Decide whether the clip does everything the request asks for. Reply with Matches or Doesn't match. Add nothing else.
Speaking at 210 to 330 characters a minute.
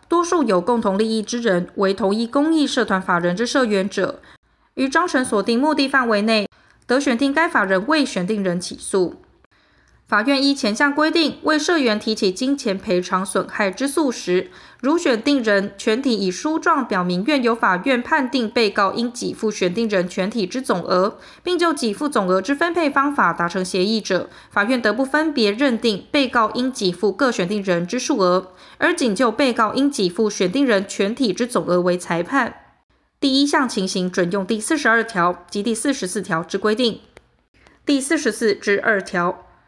Matches